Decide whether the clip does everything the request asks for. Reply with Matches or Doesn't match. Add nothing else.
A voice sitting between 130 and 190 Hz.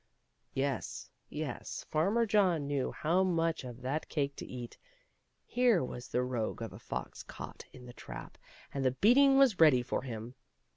Matches